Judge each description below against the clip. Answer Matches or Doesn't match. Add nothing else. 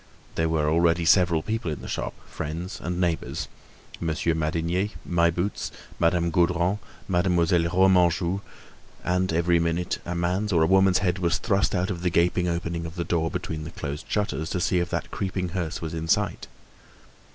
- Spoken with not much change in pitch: Matches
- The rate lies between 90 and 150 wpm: Doesn't match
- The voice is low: Matches